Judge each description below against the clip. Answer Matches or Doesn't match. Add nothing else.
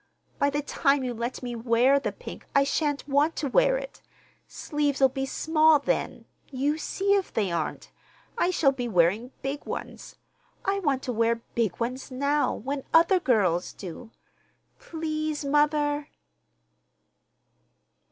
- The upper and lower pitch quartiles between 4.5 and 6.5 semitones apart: Doesn't match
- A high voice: Matches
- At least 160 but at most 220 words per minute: Doesn't match